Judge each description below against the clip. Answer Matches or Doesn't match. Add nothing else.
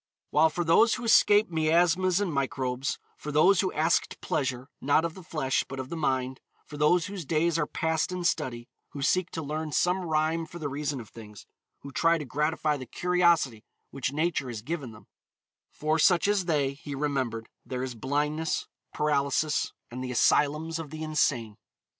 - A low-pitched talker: Doesn't match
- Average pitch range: Matches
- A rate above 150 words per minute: Matches